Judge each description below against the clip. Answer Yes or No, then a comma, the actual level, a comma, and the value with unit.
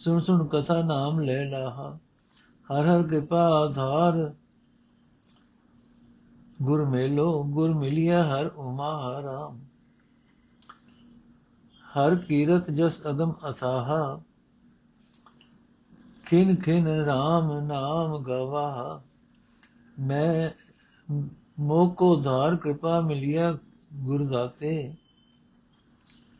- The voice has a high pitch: No, medium, 150 Hz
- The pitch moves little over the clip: No, average, 3.1 semitones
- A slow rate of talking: Yes, slow, 75 wpm